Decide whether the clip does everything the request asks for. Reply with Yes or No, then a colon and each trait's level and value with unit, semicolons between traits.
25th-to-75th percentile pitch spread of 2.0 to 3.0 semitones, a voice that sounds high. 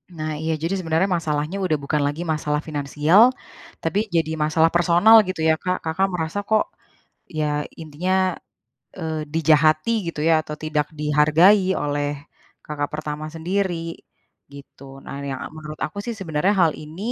No: narrow, 2.6 semitones; medium, 160 Hz